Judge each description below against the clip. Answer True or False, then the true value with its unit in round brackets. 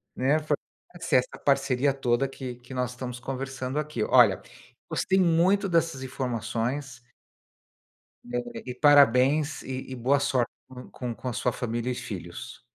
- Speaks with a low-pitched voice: True (130 Hz)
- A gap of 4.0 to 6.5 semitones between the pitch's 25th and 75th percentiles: False (2.8 semitones)